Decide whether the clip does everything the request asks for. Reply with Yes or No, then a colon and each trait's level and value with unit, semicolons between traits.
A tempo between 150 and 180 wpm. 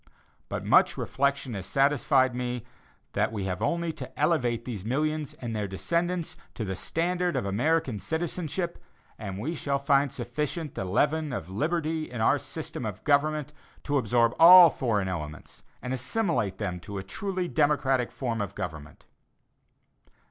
Yes: average, 155 wpm